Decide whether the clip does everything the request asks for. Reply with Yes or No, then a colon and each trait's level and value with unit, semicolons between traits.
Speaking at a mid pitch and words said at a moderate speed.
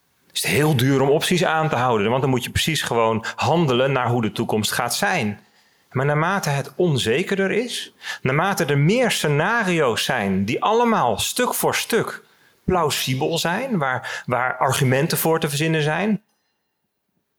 Yes: medium, 150 Hz; average, 160 wpm